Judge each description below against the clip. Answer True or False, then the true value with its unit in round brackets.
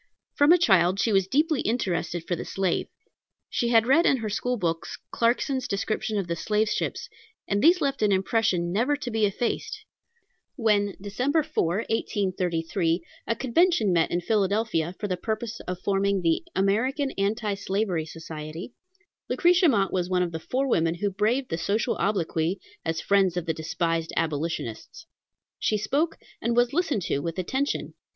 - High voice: True (200 Hz)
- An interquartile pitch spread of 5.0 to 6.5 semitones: True (5.5 semitones)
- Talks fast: False (165 wpm)